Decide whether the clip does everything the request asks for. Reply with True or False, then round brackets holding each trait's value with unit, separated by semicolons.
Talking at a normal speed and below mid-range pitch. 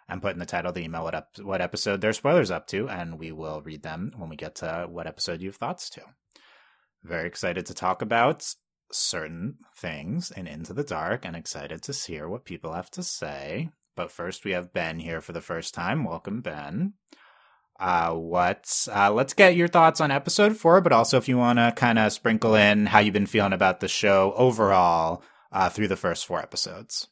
False (210 wpm; 105 Hz)